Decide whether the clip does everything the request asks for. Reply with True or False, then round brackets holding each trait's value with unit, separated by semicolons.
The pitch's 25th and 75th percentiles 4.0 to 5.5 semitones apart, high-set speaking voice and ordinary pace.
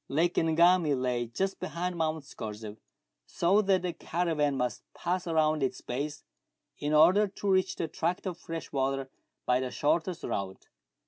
False (4.7 semitones; 160 Hz; 155 wpm)